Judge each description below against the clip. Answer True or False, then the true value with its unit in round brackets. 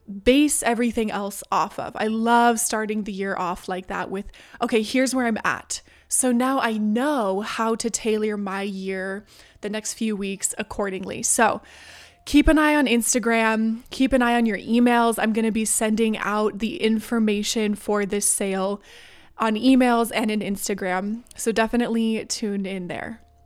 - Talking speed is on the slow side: False (170 wpm)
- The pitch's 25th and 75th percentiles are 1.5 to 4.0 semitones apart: True (2.6 semitones)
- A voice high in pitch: True (220 Hz)